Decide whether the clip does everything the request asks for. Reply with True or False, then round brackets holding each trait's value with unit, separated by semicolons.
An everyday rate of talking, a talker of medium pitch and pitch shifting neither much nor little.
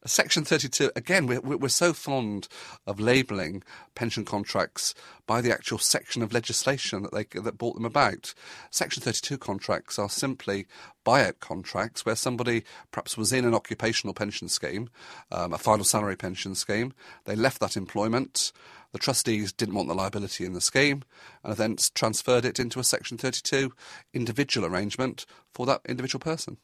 False (160 wpm; 115 Hz; 4.1 semitones)